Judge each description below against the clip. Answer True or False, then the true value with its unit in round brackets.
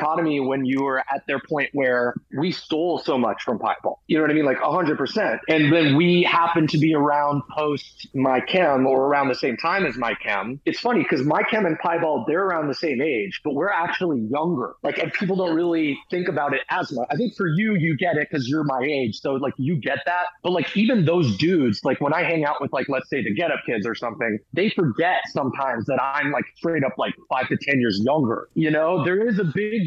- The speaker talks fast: True (245 wpm)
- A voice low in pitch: False (155 Hz)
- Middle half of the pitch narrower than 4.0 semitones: False (4.3 semitones)